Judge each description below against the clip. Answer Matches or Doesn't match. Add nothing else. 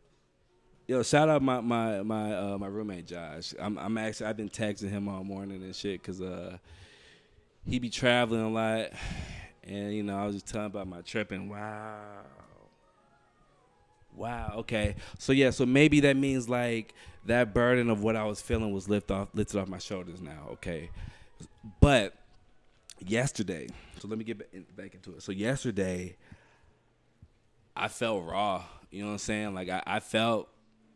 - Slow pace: Doesn't match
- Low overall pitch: Matches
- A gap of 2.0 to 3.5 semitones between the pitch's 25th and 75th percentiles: Matches